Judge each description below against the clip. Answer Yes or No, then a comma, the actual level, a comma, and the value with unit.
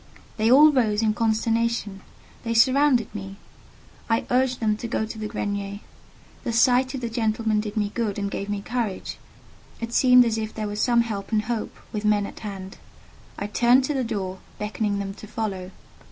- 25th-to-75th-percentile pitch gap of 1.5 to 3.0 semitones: Yes, narrow, 2.5 semitones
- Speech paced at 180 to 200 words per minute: Yes, average, 190 wpm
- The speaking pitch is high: Yes, high, 220 Hz